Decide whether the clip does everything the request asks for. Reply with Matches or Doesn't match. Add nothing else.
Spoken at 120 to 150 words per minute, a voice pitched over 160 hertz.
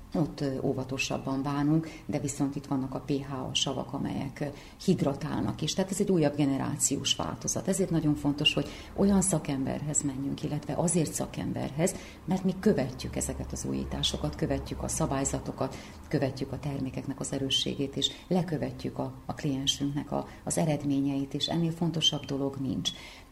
Doesn't match